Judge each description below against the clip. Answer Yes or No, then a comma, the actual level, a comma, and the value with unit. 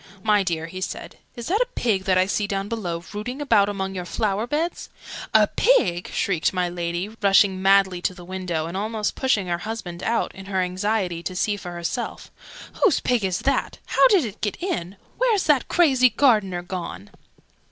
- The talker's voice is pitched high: Yes, high, 195 Hz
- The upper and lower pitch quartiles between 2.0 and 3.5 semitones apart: No, average, 4.1 semitones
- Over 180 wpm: Yes, average, 190 wpm